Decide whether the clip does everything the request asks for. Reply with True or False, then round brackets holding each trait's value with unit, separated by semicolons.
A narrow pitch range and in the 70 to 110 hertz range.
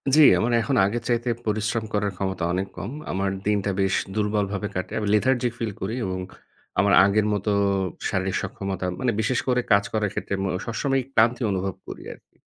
False (3.0 semitones; 105 Hz)